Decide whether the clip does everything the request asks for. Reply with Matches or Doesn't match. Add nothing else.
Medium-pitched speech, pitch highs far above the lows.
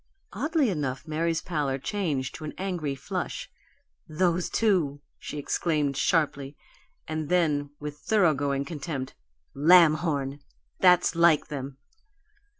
Doesn't match